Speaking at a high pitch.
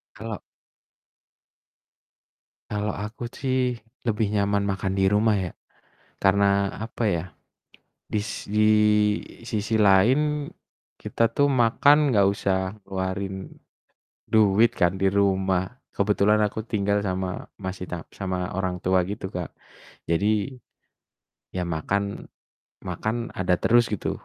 No: low, 100 Hz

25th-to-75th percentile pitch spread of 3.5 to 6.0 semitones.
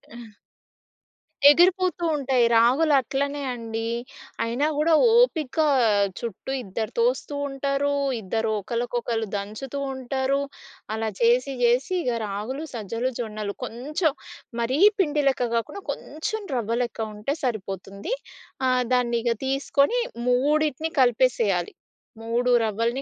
Yes: average, 4.0 semitones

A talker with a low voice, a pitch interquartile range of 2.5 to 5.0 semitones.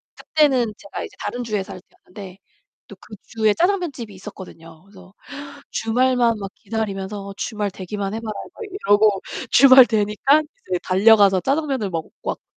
No: high, 210 Hz; average, 4.3 semitones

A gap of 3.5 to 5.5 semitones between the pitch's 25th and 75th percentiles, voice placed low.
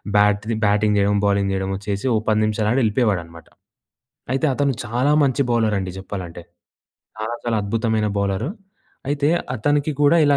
Yes: average, 3.9 semitones; low, 110 Hz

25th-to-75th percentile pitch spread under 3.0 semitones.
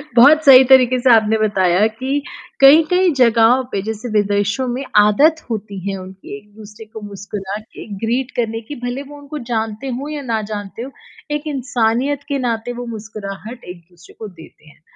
No: average, 4.2 semitones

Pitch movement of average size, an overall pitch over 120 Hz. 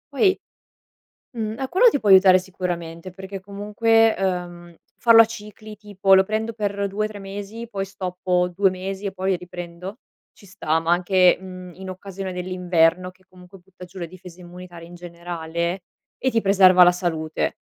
No: narrow, 2.2 semitones; medium, 185 Hz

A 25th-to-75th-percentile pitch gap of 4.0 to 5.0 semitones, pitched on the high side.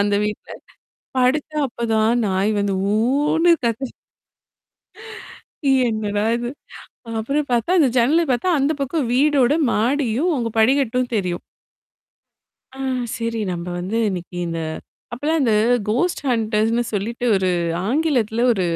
Yes: average, 4.3 semitones; high, 235 Hz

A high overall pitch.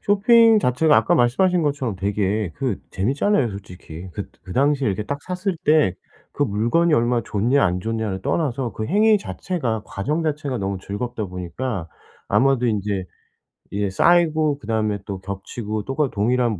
No: low, 120 Hz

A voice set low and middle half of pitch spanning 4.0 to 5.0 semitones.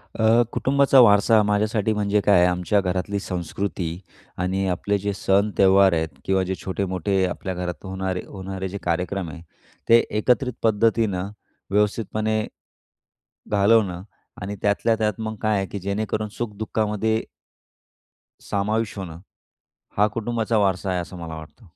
No: low, 100 Hz; narrow, 2.6 semitones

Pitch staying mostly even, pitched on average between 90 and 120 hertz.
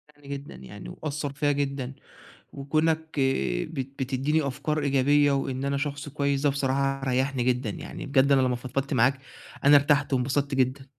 No: narrow, 1.5 semitones; medium, 140 Hz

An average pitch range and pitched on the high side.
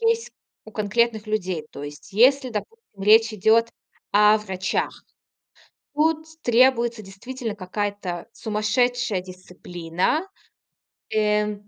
Yes: average, 3.7 semitones; high, 215 Hz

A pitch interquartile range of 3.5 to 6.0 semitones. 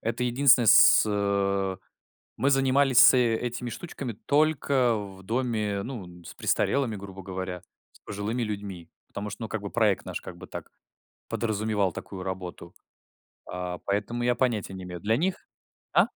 Yes: average, 4.1 semitones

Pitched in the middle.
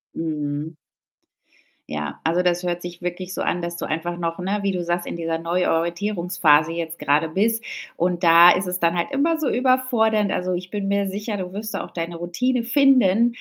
Yes: medium, 180 Hz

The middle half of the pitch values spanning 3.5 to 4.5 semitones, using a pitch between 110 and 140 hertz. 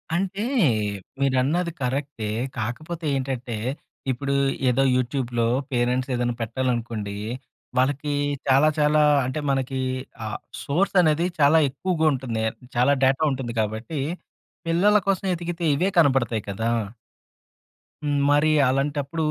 Yes: average, 4.1 semitones; low, 135 Hz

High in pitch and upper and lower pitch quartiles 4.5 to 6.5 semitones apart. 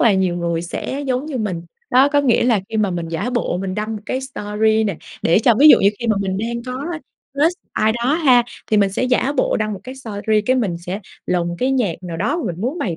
Yes: high, 220 Hz; average, 5.0 semitones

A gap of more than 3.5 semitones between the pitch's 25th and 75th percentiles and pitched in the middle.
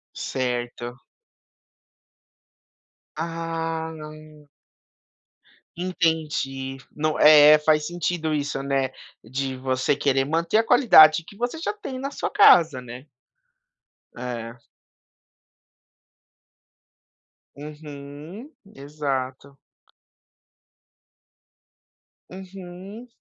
Yes: average, 3.9 semitones; medium, 155 Hz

